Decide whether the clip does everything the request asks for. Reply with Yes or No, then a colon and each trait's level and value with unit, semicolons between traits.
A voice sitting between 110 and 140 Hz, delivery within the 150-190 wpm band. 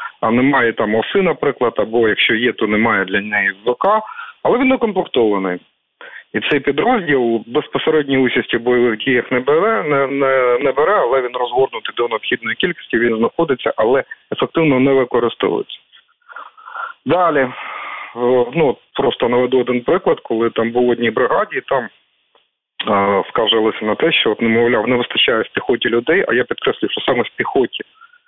Yes: low, 135 Hz; fast, 155 wpm